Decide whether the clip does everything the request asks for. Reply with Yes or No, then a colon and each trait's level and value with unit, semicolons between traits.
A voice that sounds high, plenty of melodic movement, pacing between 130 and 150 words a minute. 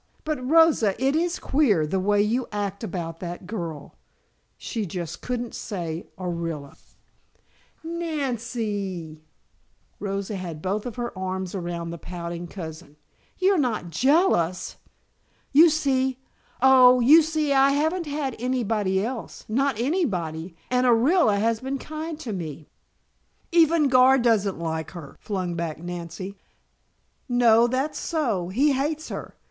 Yes: high, 220 Hz; wide, 7.4 semitones; slow, 135 wpm